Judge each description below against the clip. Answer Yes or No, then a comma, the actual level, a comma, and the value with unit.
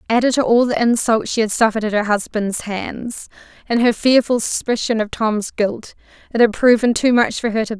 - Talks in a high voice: Yes, high, 225 Hz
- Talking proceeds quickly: Yes, fast, 215 wpm